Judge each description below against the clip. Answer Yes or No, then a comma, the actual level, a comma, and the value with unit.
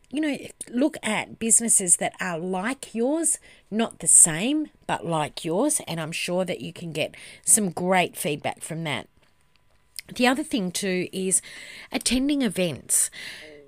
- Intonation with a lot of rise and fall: Yes, wide, 7.1 semitones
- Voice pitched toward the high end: Yes, high, 195 Hz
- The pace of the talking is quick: No, average, 150 wpm